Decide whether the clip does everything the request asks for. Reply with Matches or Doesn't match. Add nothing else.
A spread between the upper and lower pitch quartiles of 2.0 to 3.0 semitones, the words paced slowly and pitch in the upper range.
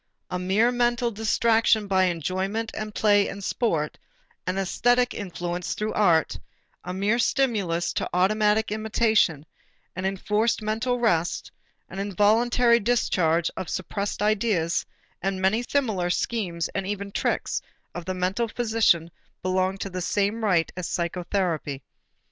Doesn't match